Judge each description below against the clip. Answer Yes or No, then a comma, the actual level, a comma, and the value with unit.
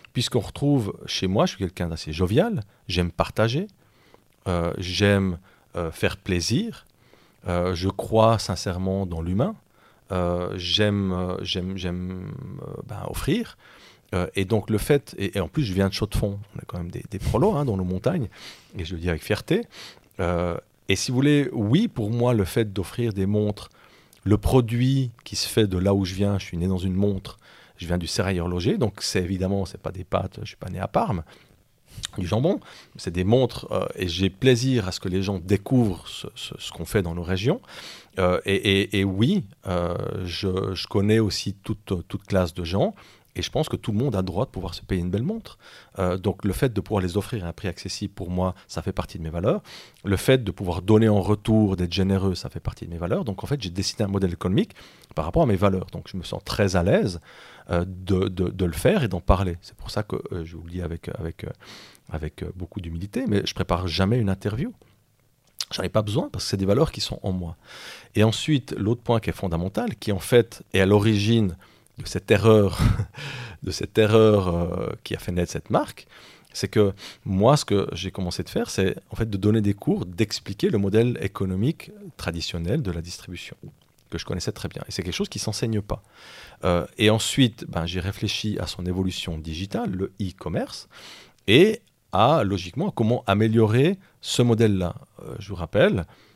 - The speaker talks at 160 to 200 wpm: No, average, 215 wpm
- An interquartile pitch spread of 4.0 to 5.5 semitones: No, average, 3.4 semitones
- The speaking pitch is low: Yes, low, 100 Hz